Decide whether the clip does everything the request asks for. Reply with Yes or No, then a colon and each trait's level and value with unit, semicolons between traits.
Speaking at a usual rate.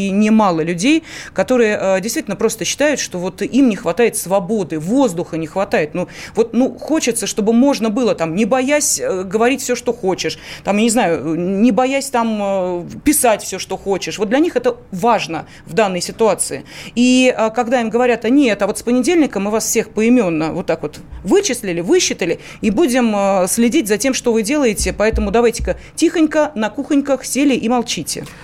No: fast, 175 wpm